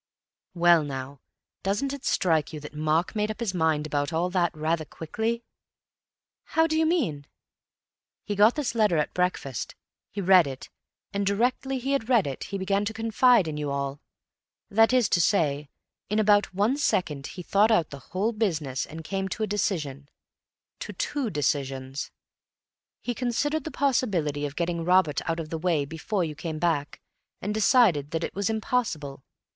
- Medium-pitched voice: Yes, medium, 180 Hz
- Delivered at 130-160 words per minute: No, average, 175 wpm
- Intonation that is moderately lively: No, wide, 6.3 semitones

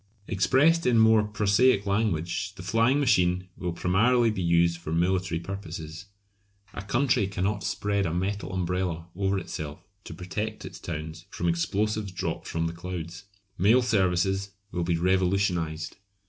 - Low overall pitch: Yes, very low, 95 Hz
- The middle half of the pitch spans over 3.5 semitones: No, average, 3.2 semitones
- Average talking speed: Yes, average, 145 wpm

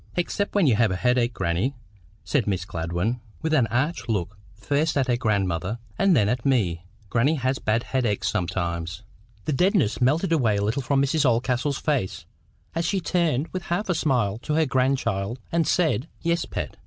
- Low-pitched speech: Yes, low, 125 Hz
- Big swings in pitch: Yes, wide, 6.8 semitones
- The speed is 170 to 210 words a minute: Yes, average, 180 wpm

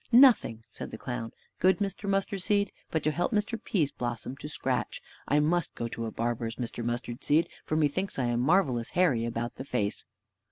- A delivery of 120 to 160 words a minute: No, average, 195 wpm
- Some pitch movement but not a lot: No, wide, 7.9 semitones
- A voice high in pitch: No, medium, 145 Hz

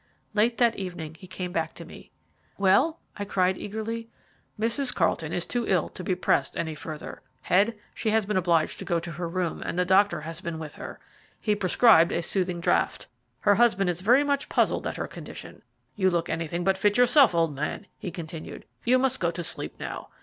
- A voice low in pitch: No, medium, 185 Hz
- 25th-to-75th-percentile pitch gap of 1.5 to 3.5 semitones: No, average, 4.5 semitones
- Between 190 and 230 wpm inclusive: Yes, fast, 205 wpm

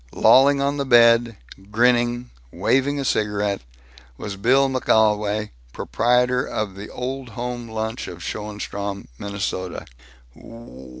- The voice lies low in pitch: Yes, low, 115 Hz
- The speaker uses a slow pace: Yes, slow, 110 wpm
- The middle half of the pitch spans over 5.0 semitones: No, average, 3.2 semitones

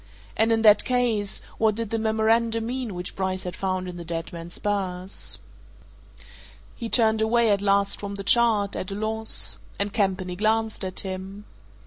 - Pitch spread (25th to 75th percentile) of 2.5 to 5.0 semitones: Yes, average, 2.9 semitones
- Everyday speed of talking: Yes, average, 170 wpm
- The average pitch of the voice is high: Yes, high, 205 Hz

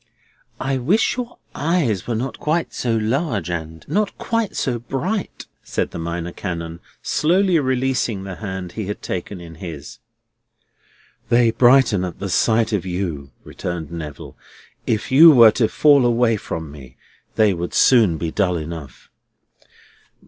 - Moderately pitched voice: No, low, 110 Hz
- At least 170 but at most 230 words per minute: No, average, 150 wpm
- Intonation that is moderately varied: No, wide, 7.5 semitones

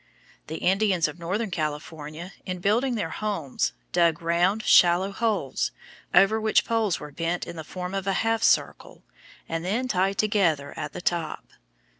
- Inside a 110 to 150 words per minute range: No, average, 160 wpm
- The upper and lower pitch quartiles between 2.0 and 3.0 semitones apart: No, average, 4.2 semitones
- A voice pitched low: No, medium, 180 Hz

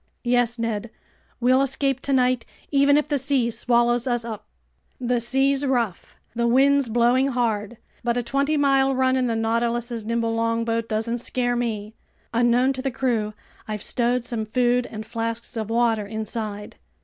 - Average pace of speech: Yes, average, 160 wpm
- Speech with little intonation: Yes, narrow, 2.2 semitones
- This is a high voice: Yes, high, 240 Hz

